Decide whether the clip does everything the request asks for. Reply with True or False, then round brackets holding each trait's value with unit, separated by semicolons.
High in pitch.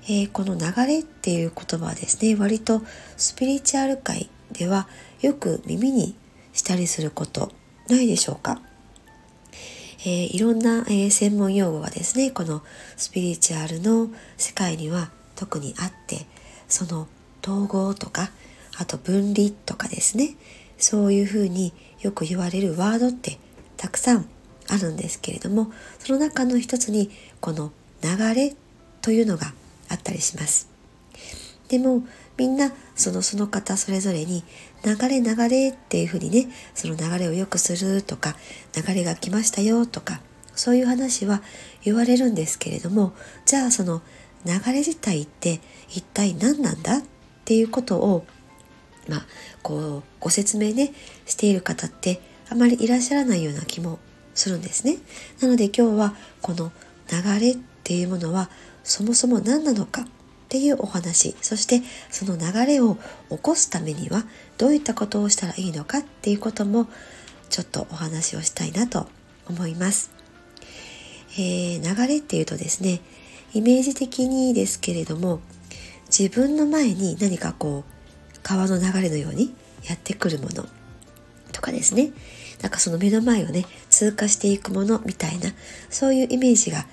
True (200 Hz)